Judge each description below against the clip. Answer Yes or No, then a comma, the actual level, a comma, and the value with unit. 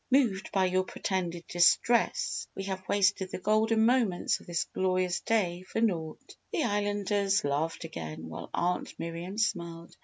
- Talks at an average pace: Yes, average, 150 wpm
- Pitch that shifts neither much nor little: Yes, average, 3.1 semitones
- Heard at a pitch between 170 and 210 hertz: Yes, medium, 185 Hz